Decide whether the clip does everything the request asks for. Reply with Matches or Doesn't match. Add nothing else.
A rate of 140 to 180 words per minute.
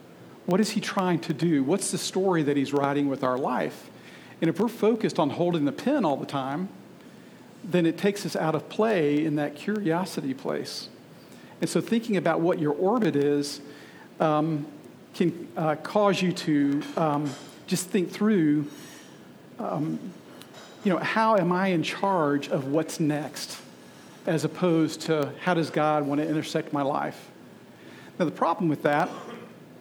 Matches